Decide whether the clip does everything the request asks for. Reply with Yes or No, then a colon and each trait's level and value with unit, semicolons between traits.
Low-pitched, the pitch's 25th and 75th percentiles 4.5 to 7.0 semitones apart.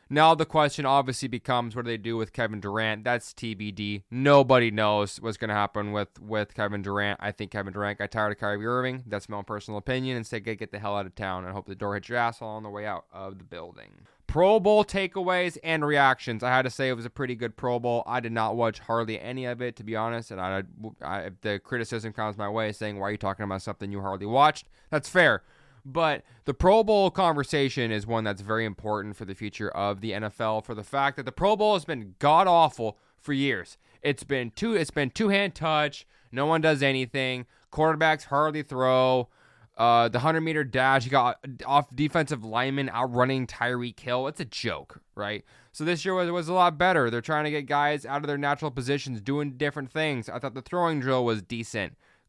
Yes: low, 120 Hz; average, 5.1 semitones